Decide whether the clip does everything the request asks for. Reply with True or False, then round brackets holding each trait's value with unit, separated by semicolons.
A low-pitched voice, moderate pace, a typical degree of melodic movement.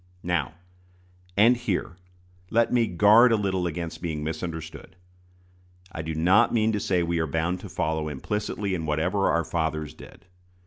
True (85 Hz; 155 wpm; 4.6 semitones)